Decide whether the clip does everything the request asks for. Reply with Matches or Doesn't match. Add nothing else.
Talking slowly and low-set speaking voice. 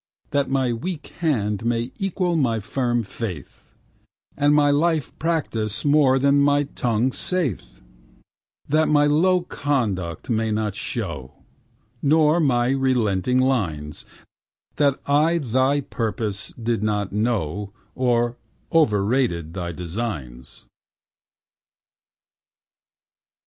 Matches